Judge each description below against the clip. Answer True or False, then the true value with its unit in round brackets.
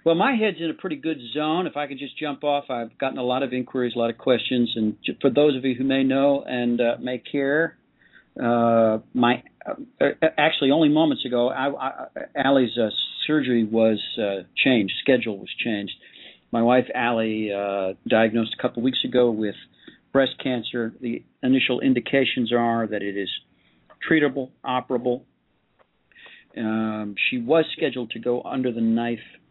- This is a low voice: True (125 Hz)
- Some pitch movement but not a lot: True (3.2 semitones)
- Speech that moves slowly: False (175 wpm)